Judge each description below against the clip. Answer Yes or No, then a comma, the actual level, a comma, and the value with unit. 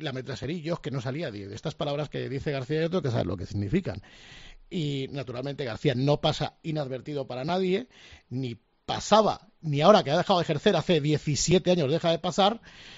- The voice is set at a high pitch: No, medium, 150 Hz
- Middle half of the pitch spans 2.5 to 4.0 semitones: No, average, 4.6 semitones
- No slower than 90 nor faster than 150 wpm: No, average, 180 wpm